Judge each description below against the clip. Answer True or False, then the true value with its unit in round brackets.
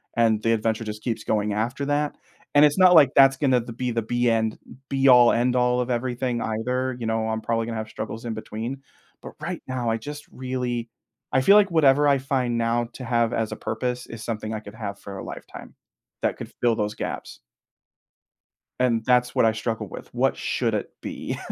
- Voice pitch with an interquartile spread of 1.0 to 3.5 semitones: True (2.6 semitones)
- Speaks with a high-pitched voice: False (120 Hz)